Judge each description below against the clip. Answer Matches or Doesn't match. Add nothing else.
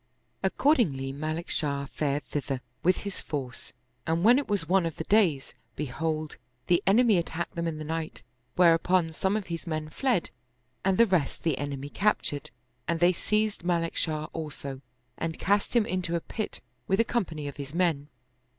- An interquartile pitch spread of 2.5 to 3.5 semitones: Doesn't match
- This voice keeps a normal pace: Matches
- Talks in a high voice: Doesn't match